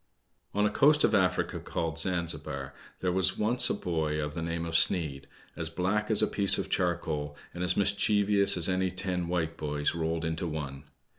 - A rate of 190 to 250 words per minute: Yes, average, 195 wpm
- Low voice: Yes, very low, 85 Hz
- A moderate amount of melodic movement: Yes, average, 3.1 semitones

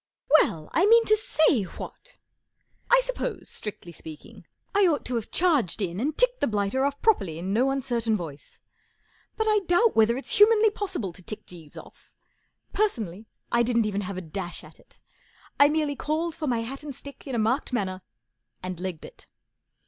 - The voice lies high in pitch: Yes, very high, 250 Hz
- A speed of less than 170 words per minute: No, average, 185 wpm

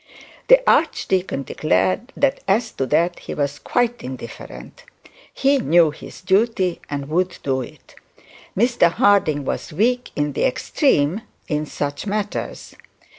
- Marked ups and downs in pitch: Yes, wide, 8.1 semitones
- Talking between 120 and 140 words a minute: Yes, slow, 135 wpm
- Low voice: No, medium, 180 Hz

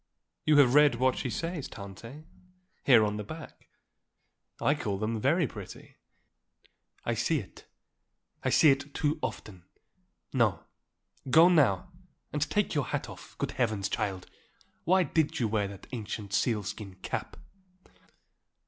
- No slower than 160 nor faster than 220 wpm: No, average, 140 wpm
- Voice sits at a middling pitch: No, low, 120 Hz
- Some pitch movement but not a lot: No, wide, 6.3 semitones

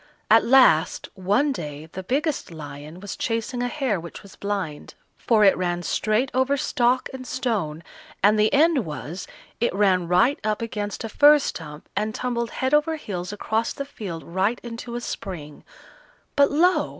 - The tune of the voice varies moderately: No, wide, 6.3 semitones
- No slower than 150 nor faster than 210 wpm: Yes, average, 170 wpm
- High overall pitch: Yes, high, 215 Hz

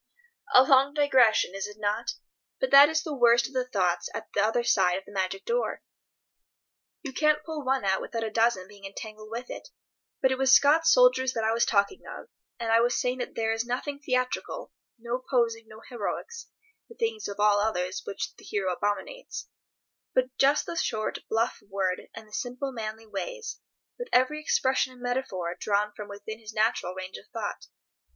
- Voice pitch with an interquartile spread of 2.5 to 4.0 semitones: No, average, 4.4 semitones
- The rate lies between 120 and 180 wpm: No, average, 190 wpm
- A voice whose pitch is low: No, high, 235 Hz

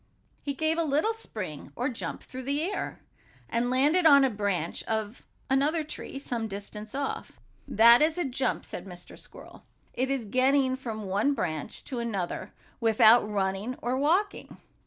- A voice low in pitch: No, very high, 255 Hz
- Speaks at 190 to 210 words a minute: No, average, 160 wpm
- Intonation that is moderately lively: Yes, average, 5.0 semitones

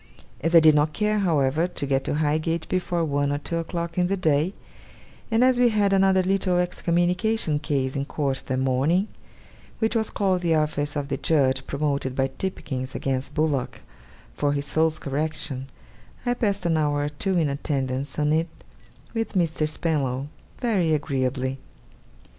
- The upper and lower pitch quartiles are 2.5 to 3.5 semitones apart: No, average, 4.3 semitones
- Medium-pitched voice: Yes, medium, 155 Hz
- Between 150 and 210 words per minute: Yes, average, 165 wpm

